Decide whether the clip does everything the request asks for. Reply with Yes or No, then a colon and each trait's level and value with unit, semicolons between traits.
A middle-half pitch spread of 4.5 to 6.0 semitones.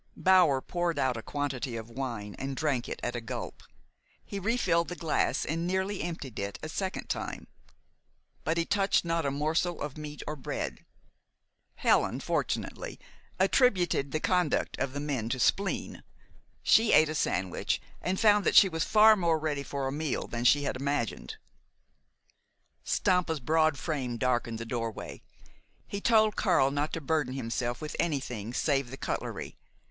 Yes: average, 5.2 semitones